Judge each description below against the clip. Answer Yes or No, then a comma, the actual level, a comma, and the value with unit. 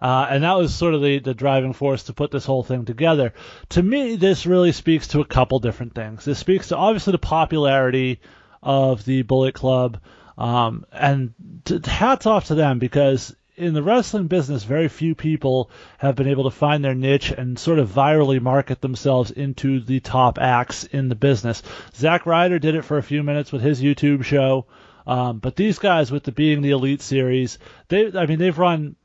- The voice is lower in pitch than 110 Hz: No, medium, 140 Hz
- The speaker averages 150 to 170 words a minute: No, average, 200 wpm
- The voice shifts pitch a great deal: No, average, 3.7 semitones